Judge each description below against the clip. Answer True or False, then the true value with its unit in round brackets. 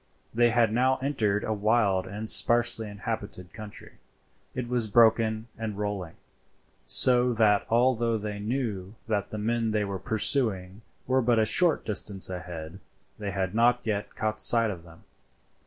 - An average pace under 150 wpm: False (155 wpm)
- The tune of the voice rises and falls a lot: False (2.7 semitones)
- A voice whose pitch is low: True (110 Hz)